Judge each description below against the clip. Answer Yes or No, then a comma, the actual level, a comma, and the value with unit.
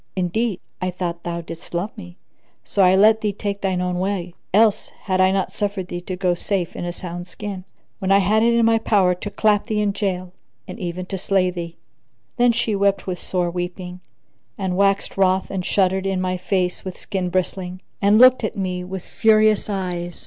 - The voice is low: No, high, 190 Hz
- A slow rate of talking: No, fast, 205 wpm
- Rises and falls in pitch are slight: Yes, narrow, 2.1 semitones